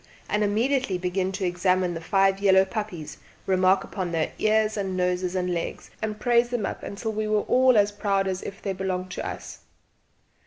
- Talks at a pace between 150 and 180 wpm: No, average, 195 wpm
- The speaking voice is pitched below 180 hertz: No, high, 195 Hz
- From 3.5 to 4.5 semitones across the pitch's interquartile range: No, narrow, 2.6 semitones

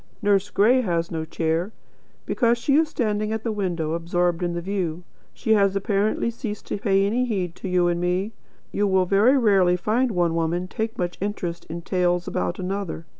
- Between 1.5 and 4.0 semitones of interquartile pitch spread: Yes, average, 3.4 semitones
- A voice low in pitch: No, high, 190 Hz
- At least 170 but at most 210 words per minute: Yes, average, 190 wpm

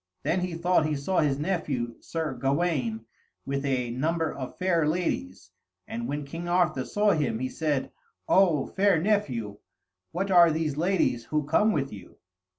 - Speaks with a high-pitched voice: No, medium, 150 Hz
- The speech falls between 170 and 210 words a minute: No, average, 160 wpm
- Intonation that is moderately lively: Yes, average, 5.0 semitones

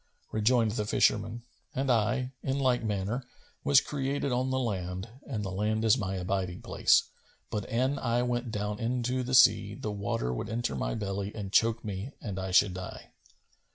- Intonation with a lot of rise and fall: No, average, 4.1 semitones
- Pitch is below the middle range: Yes, low, 110 Hz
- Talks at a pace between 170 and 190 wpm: Yes, average, 180 wpm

